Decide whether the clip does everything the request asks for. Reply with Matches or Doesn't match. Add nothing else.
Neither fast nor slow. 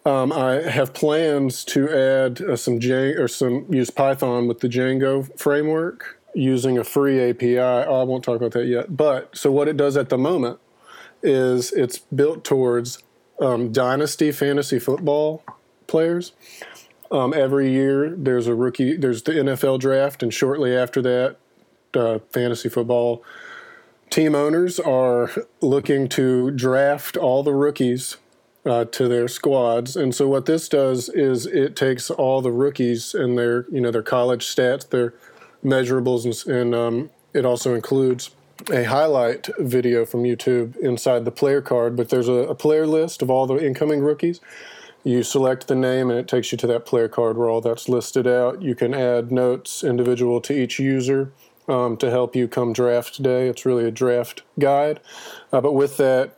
Matches